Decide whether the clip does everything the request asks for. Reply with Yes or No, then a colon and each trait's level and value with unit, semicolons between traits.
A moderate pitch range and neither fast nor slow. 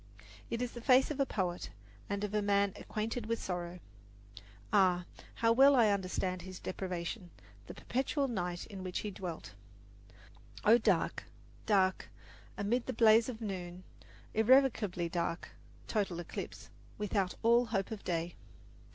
Yes: average, 4.1 semitones; average, 145 wpm